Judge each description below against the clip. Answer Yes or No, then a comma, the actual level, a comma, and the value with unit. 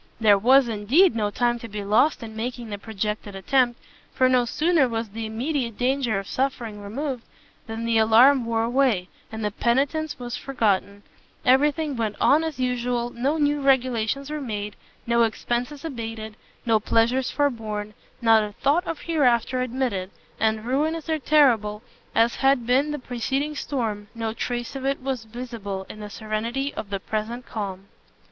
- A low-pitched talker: No, high, 235 Hz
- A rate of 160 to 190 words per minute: Yes, average, 165 wpm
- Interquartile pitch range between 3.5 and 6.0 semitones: Yes, average, 3.8 semitones